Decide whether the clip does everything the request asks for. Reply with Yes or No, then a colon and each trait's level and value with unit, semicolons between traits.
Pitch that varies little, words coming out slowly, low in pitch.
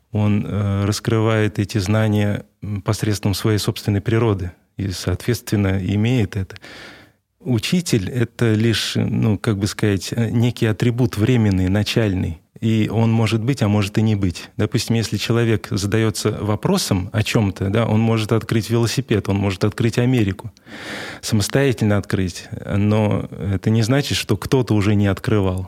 No: narrow, 2.2 semitones; average, 140 wpm; low, 110 Hz